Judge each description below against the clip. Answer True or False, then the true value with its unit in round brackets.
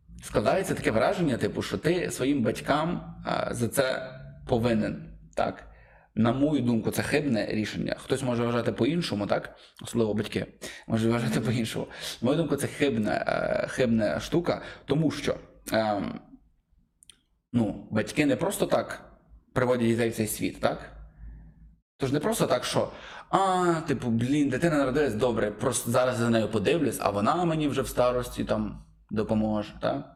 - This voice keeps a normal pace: True (145 wpm)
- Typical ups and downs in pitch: True (3.6 semitones)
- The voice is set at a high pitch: False (115 Hz)